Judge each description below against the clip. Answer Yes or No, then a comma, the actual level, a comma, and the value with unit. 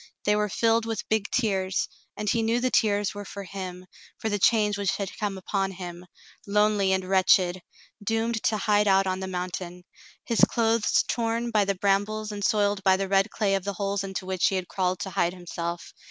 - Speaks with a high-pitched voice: Yes, high, 200 Hz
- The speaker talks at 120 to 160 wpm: No, fast, 205 wpm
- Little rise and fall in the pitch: Yes, narrow, 2.1 semitones